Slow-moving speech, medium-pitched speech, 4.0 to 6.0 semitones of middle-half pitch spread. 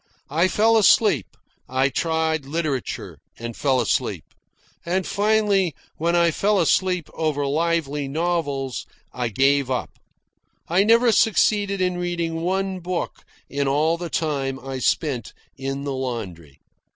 Yes: slow, 130 wpm; medium, 160 Hz; average, 5.1 semitones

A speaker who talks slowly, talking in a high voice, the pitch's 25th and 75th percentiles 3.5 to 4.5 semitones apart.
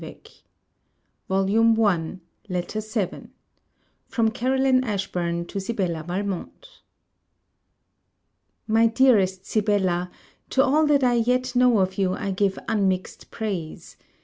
Yes: slow, 105 wpm; high, 205 Hz; average, 4.1 semitones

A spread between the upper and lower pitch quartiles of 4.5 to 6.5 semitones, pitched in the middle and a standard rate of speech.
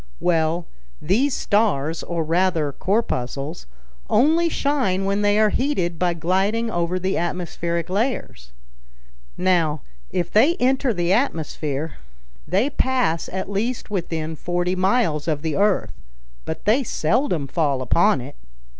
No: average, 5.0 semitones; medium, 180 Hz; slow, 130 wpm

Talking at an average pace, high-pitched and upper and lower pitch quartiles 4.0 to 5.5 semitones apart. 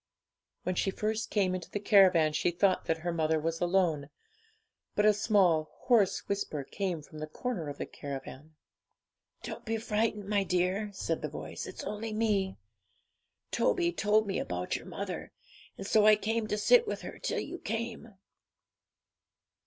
Yes: average, 165 wpm; high, 195 Hz; average, 4.6 semitones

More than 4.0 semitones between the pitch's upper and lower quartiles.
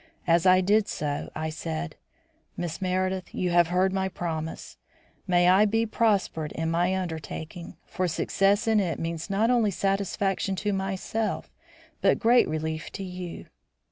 No: average, 3.0 semitones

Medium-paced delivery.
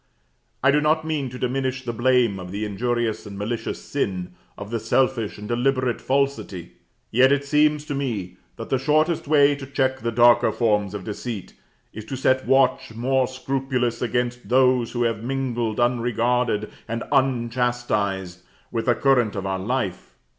Yes: average, 165 wpm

